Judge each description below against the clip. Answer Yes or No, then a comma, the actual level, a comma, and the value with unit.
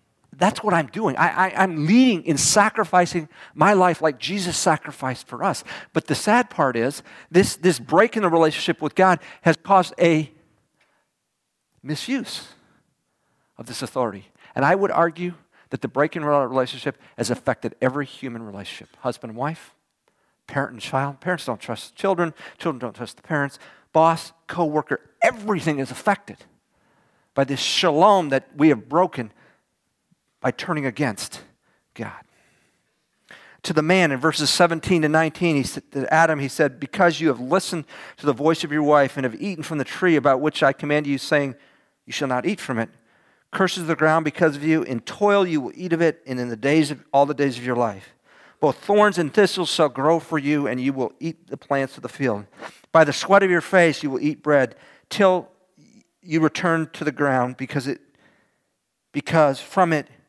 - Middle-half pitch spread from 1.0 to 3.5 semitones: No, average, 4.1 semitones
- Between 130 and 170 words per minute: No, average, 190 wpm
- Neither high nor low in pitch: Yes, medium, 155 Hz